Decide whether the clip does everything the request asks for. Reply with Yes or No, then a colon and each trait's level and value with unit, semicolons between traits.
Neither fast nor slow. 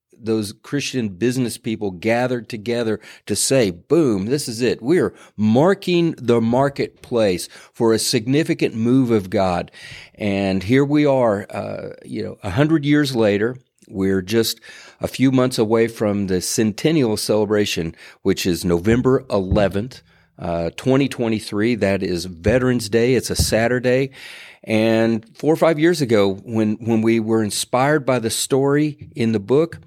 Yes: average, 145 wpm